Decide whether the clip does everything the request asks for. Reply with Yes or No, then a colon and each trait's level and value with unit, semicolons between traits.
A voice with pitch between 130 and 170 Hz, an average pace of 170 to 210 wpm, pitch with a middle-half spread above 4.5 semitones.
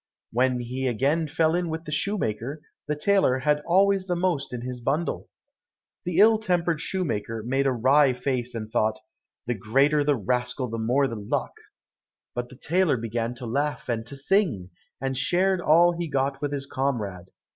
Yes: low, 135 Hz; average, 180 wpm; average, 5.1 semitones